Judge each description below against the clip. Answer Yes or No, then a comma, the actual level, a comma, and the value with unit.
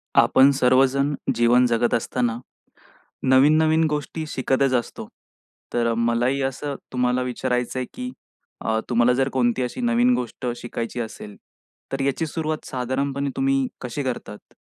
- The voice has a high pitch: No, low, 130 Hz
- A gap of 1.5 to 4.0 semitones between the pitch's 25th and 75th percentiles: Yes, narrow, 2.4 semitones